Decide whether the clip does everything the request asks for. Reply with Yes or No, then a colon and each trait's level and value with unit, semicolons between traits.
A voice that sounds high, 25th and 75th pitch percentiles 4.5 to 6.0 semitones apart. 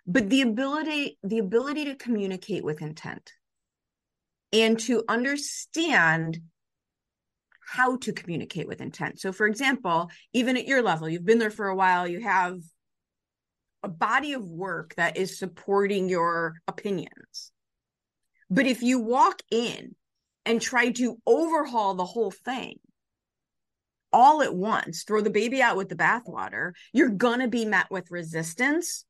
Yes: high, 220 Hz; wide, 5.6 semitones